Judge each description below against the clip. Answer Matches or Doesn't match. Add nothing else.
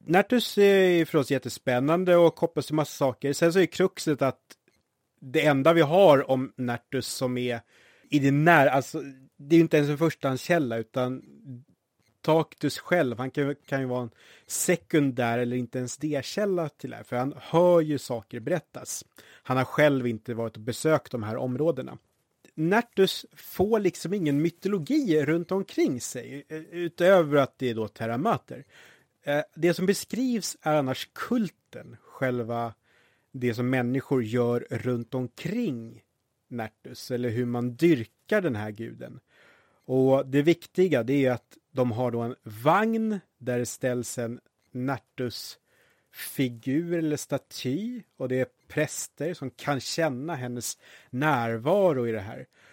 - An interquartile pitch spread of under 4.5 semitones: Doesn't match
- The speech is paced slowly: Doesn't match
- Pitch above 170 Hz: Doesn't match